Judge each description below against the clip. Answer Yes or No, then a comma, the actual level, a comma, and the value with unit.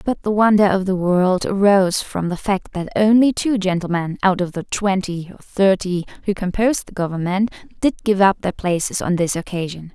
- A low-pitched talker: No, high, 190 Hz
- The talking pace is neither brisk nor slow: Yes, average, 195 wpm